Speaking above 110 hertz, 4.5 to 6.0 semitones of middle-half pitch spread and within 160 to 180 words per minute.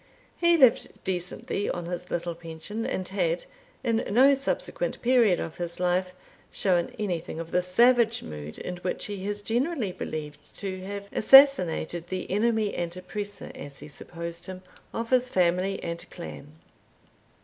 No: medium, 185 Hz; average, 4.8 semitones; average, 150 wpm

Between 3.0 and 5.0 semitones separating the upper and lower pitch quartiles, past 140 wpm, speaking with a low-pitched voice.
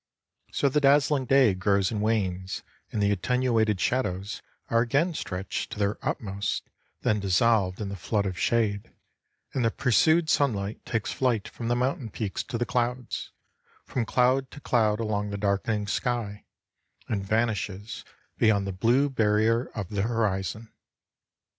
Yes: average, 3.6 semitones; average, 150 wpm; low, 110 Hz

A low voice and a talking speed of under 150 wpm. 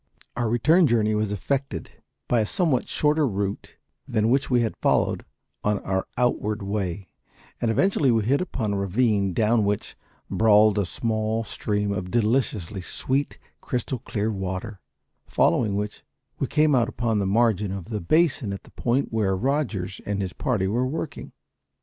No: low, 110 Hz; average, 165 wpm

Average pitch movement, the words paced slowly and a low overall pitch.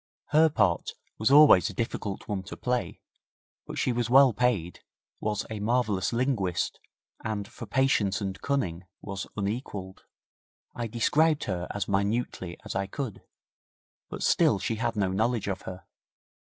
No: average, 4.2 semitones; average, 150 wpm; low, 105 Hz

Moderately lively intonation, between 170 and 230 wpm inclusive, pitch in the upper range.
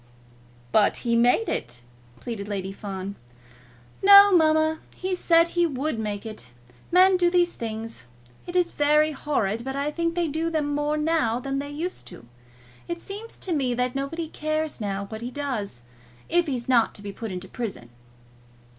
No: wide, 7.1 semitones; average, 175 wpm; very high, 280 Hz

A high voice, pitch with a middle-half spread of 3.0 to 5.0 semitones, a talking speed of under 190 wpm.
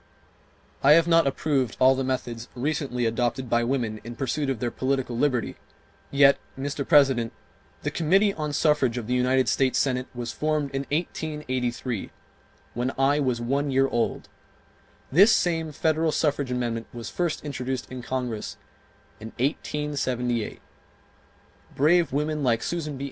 No: low, 135 Hz; average, 3.4 semitones; average, 145 wpm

